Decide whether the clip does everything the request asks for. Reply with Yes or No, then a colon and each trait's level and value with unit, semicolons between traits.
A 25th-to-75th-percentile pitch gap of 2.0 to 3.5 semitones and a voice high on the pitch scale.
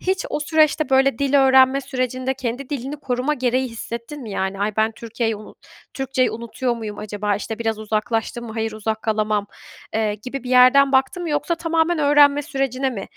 No: average, 3.9 semitones; very high, 255 Hz